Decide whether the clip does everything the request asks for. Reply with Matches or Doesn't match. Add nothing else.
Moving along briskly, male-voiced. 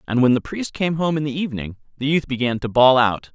Matches